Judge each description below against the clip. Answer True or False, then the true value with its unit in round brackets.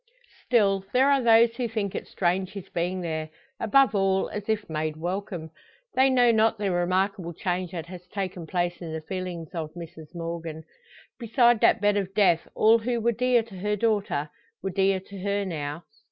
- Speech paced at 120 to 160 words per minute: False (185 wpm)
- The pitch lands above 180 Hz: True (190 Hz)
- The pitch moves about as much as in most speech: True (4.1 semitones)